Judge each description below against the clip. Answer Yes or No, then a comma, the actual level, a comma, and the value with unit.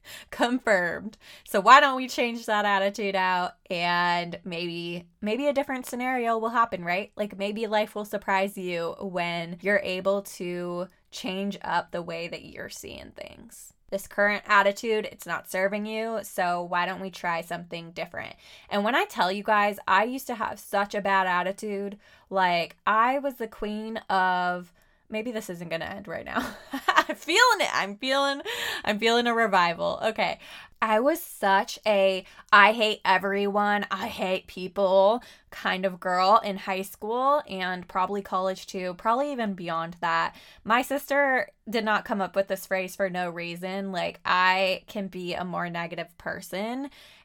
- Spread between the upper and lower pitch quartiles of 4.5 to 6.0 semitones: No, average, 3.5 semitones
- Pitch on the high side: Yes, high, 200 Hz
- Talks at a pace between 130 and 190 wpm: Yes, average, 170 wpm